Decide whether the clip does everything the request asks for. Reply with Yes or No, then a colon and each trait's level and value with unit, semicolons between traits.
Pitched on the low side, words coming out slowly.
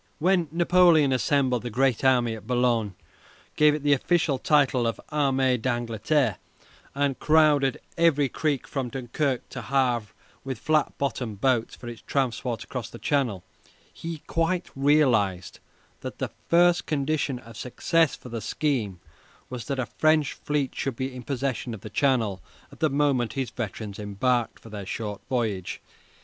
No: low, 130 Hz; average, 160 wpm